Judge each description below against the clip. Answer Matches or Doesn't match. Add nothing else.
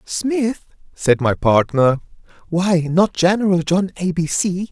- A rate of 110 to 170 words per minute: Matches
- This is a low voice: Doesn't match